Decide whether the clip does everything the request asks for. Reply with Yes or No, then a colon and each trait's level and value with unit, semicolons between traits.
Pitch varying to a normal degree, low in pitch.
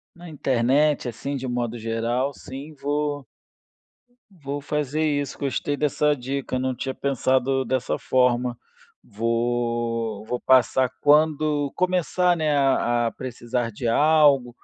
Yes: average, 3.3 semitones; low, 130 Hz